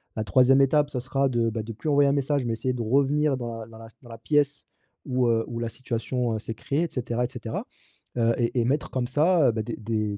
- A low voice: Yes, low, 125 Hz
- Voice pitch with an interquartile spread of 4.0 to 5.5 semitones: No, average, 3.2 semitones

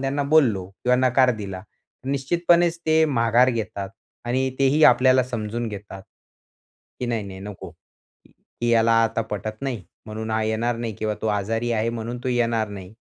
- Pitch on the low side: Yes, low, 115 Hz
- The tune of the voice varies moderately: Yes, average, 3.0 semitones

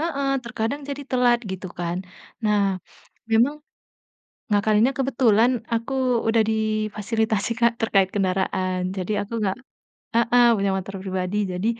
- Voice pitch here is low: No, high, 215 Hz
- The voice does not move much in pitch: No, average, 3.6 semitones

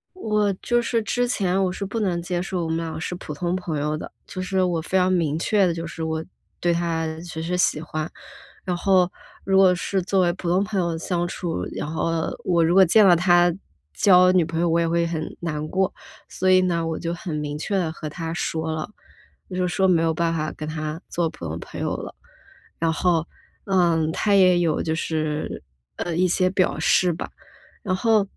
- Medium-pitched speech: Yes, medium, 175 Hz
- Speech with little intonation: Yes, narrow, 2.3 semitones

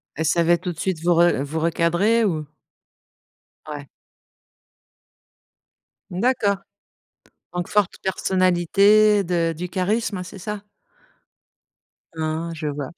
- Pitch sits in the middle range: Yes, medium, 175 Hz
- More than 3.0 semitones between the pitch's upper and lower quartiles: Yes, average, 3.5 semitones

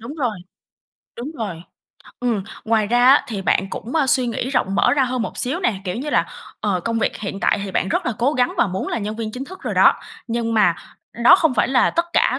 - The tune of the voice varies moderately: Yes, average, 3.7 semitones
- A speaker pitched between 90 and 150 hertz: No, high, 235 Hz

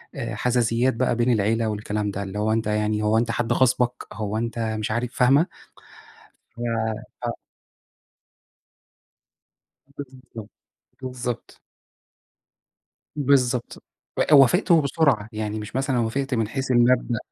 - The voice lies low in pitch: Yes, low, 120 Hz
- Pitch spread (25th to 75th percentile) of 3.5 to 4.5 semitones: No, average, 2.9 semitones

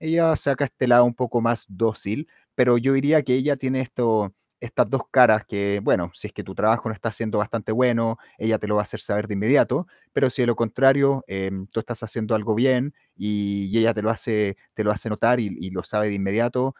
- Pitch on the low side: Yes, low, 115 Hz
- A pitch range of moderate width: Yes, average, 3.3 semitones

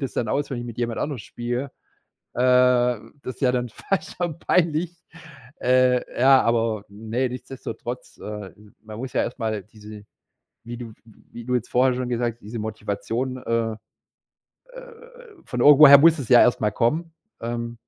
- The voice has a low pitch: Yes, low, 120 Hz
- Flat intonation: Yes, narrow, 2.3 semitones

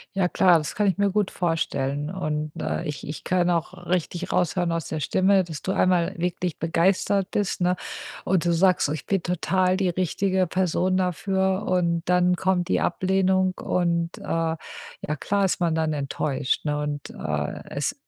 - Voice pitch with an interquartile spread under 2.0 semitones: No, narrow, 2.4 semitones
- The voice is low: No, medium, 180 Hz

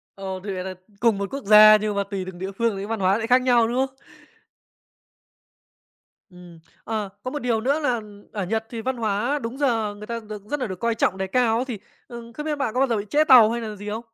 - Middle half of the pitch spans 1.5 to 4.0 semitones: Yes, average, 3.6 semitones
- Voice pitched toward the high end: Yes, high, 225 Hz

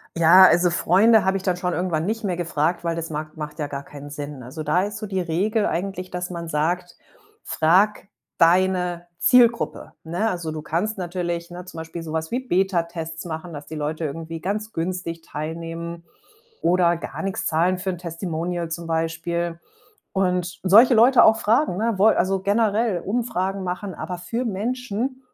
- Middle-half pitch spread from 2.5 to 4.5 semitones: Yes, average, 2.9 semitones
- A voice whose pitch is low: No, medium, 175 Hz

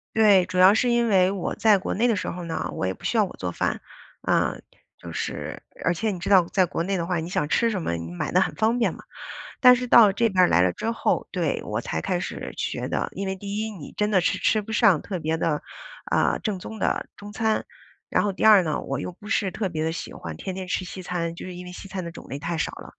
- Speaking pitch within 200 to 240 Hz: No, medium, 185 Hz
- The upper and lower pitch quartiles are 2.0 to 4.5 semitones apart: Yes, average, 4.0 semitones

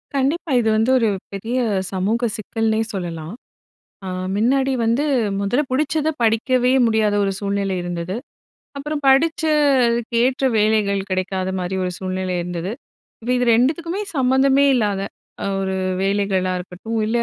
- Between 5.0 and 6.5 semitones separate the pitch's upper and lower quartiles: Yes, wide, 5.4 semitones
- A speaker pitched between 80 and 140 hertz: No, high, 225 Hz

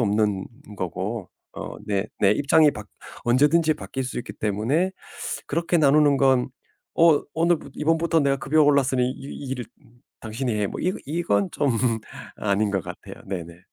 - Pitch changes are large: Yes, wide, 6.3 semitones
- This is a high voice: No, low, 130 Hz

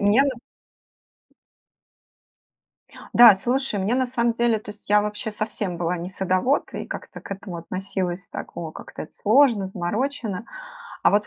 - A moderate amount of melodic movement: Yes, average, 4.1 semitones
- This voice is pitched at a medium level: No, high, 205 Hz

